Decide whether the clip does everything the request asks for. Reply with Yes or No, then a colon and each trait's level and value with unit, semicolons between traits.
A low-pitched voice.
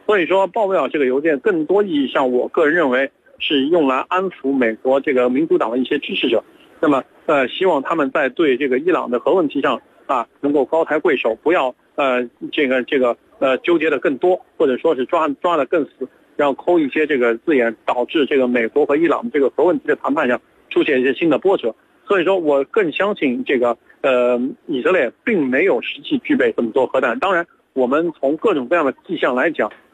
No: medium, 170 Hz